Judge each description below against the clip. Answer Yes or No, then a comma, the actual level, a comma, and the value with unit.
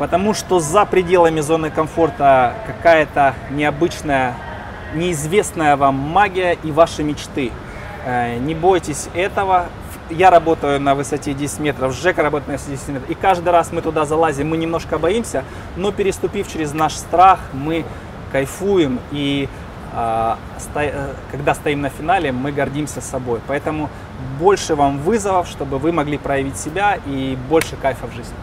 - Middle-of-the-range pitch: Yes, medium, 150 Hz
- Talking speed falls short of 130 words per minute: No, average, 140 wpm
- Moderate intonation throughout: Yes, average, 3.8 semitones